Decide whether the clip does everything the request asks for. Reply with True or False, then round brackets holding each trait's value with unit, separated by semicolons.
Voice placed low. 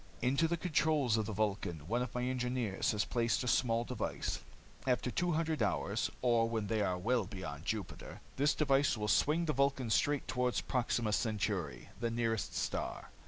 True (120 Hz)